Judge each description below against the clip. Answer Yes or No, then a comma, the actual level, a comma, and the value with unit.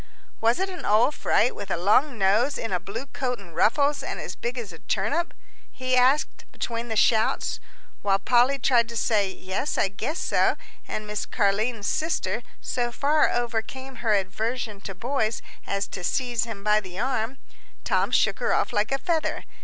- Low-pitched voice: No, high, 230 Hz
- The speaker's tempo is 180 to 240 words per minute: Yes, average, 185 wpm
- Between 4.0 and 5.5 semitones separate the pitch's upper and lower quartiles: Yes, average, 4.3 semitones